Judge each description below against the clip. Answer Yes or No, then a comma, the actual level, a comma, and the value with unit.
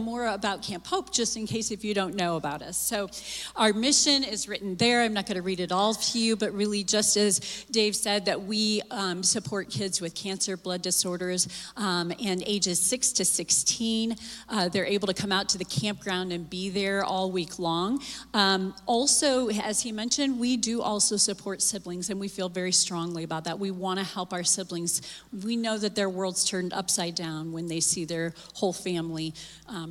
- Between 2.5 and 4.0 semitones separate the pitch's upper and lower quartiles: Yes, average, 2.9 semitones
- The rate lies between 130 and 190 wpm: No, fast, 205 wpm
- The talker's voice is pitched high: Yes, high, 195 Hz